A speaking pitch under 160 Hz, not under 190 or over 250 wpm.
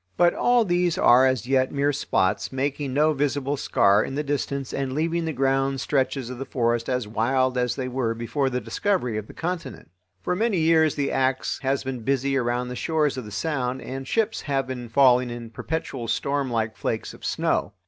Yes: low, 135 Hz; average, 200 wpm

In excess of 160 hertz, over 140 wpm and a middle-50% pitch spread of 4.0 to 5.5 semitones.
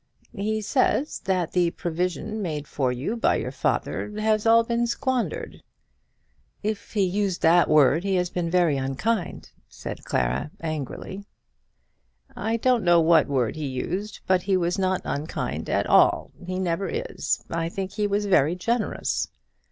Yes: medium, 185 Hz; average, 155 wpm; average, 4.5 semitones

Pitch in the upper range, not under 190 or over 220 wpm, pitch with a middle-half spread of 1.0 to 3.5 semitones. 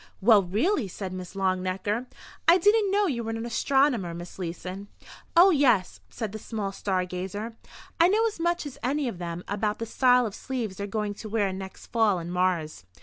No: high, 210 Hz; average, 195 wpm; wide, 5.6 semitones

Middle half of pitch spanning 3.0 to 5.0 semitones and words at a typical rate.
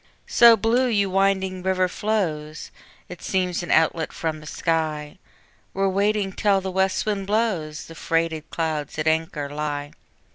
Yes: average, 3.8 semitones; average, 150 wpm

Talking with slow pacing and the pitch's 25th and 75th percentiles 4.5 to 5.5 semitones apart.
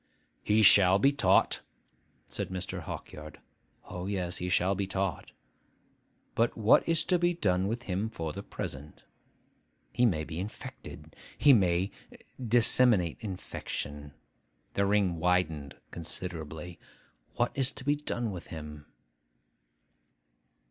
Yes: slow, 125 wpm; average, 5.1 semitones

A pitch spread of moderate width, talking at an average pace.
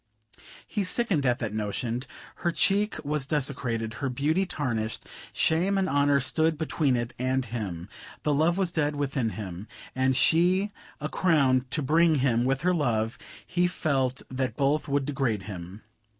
Yes: average, 4.8 semitones; average, 160 wpm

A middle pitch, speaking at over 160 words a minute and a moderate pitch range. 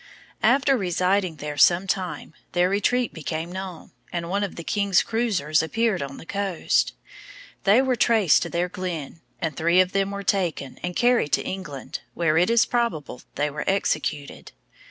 Yes: medium, 180 Hz; average, 170 wpm; average, 3.9 semitones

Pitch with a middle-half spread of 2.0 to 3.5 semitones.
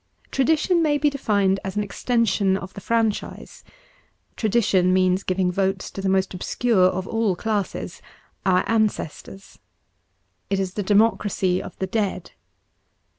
Yes: average, 3.0 semitones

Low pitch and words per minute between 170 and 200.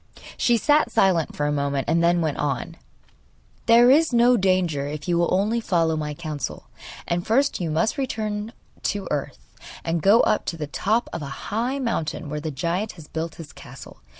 No: medium, 170 Hz; average, 190 wpm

